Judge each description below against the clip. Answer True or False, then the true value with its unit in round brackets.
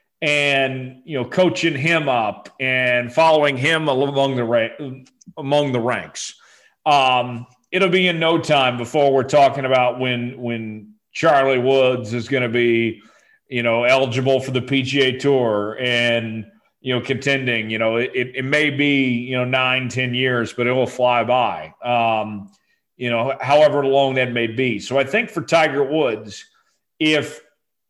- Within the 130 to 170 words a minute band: True (160 wpm)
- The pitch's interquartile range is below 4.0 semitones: True (2.8 semitones)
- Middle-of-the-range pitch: False (130 Hz)